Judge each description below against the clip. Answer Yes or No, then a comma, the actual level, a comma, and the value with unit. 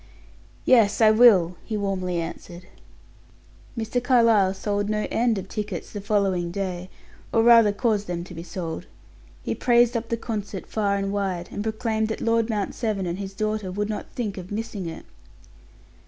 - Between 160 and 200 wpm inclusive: Yes, average, 170 wpm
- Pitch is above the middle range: Yes, high, 205 Hz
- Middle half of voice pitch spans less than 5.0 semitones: Yes, average, 3.1 semitones